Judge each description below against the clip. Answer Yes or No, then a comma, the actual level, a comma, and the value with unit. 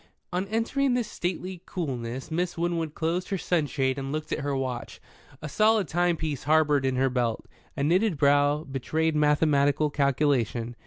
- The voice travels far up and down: No, average, 4.2 semitones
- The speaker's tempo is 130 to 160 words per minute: Yes, average, 155 wpm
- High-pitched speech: No, medium, 150 Hz